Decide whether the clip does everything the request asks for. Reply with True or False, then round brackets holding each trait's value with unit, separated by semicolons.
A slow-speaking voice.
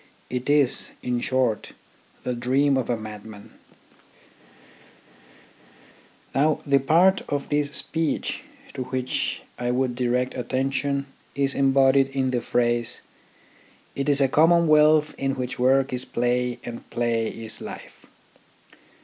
True (125 wpm)